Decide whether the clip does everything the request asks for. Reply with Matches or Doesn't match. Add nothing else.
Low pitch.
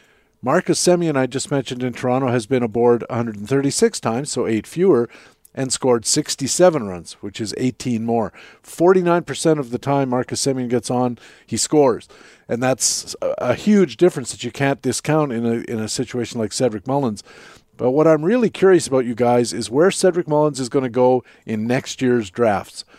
Matches